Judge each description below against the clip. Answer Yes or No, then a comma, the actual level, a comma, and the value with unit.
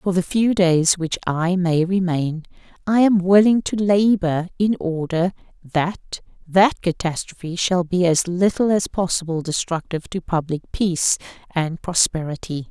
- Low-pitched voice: No, medium, 180 Hz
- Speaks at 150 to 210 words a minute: No, average, 140 wpm